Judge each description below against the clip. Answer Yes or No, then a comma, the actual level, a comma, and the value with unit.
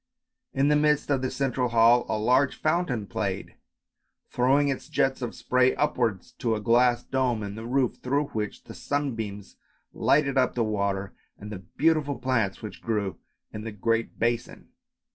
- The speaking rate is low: No, average, 165 wpm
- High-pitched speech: No, low, 125 Hz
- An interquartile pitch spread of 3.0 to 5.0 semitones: Yes, average, 4.1 semitones